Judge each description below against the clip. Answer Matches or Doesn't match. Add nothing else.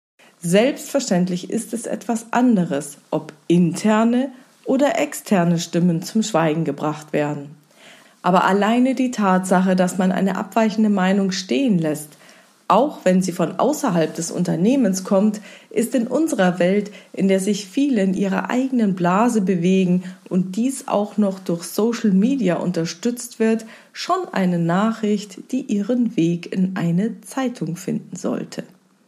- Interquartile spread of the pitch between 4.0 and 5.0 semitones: Matches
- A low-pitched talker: Doesn't match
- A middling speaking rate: Matches